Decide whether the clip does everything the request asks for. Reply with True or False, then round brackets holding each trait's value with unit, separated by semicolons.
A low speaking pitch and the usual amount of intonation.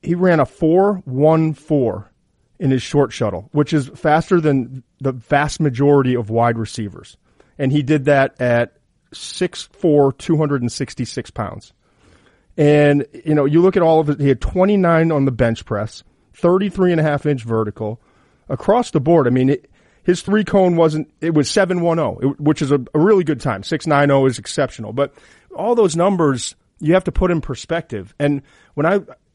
False (145 Hz; 4.2 semitones)